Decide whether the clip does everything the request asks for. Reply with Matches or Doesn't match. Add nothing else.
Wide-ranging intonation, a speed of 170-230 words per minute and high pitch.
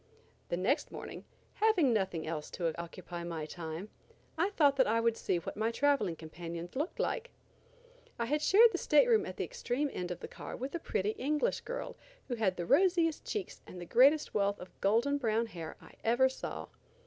Matches